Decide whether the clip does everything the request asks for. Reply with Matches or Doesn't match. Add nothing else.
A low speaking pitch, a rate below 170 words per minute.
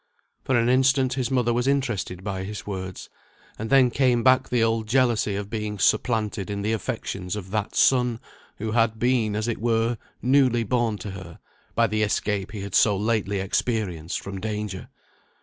Doesn't match